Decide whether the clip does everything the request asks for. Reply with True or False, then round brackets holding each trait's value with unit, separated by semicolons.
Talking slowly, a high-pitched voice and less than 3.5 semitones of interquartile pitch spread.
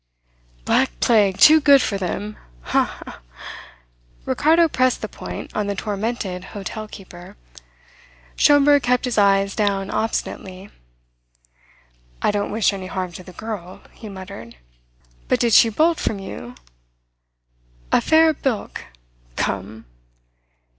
False (125 wpm; 205 Hz; 4.5 semitones)